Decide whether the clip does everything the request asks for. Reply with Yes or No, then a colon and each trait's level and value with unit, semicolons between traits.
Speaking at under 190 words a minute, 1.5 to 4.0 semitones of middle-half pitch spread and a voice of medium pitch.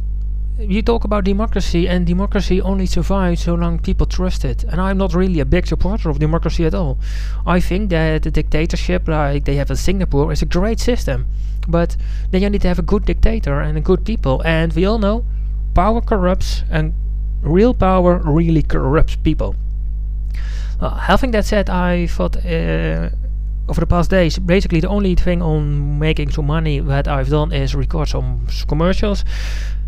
No: average, 180 wpm; average, 5.3 semitones; medium, 165 Hz